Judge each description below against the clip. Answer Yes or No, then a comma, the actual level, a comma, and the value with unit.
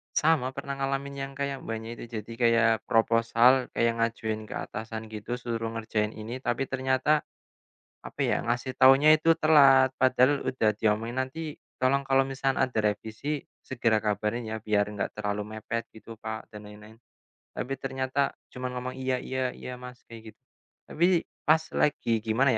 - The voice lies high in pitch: No, low, 125 Hz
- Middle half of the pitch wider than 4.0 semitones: No, average, 3.3 semitones